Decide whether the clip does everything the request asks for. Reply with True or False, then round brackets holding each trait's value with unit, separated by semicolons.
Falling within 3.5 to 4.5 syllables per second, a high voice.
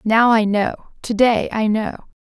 True (4.4 syllables/s; 220 Hz)